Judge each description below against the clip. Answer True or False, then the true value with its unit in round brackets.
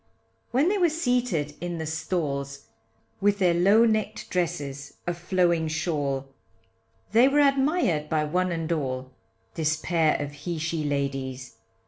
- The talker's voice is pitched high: False (165 Hz)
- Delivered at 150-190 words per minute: False (140 wpm)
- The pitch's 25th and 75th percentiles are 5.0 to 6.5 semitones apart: True (5.5 semitones)